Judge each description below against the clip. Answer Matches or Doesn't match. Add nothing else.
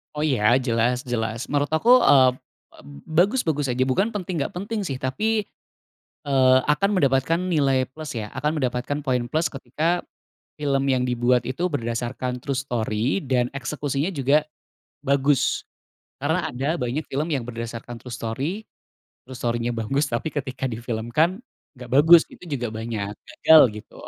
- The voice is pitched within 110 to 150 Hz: Matches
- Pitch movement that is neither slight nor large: Matches